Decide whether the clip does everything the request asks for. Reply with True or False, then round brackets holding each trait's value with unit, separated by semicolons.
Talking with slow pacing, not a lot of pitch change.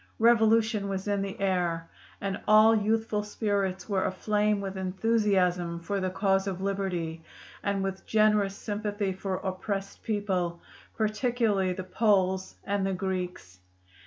True (130 wpm; 2.1 semitones)